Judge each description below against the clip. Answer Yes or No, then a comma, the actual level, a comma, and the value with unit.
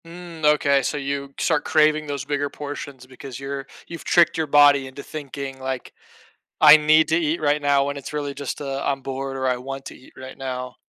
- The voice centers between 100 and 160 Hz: Yes, medium, 140 Hz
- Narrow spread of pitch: Yes, narrow, 1.9 semitones